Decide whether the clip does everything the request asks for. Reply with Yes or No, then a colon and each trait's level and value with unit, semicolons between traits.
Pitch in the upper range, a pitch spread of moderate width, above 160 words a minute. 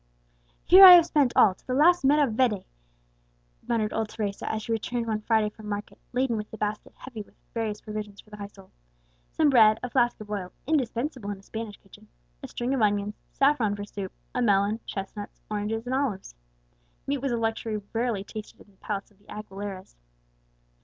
Yes: high, 220 Hz; average, 3.2 semitones; average, 190 wpm